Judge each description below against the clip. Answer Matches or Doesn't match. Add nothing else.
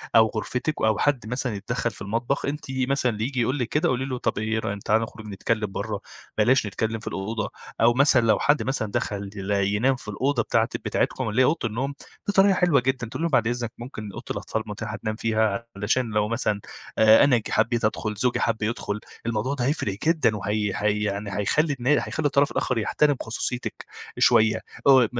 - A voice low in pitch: Matches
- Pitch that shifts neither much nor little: Matches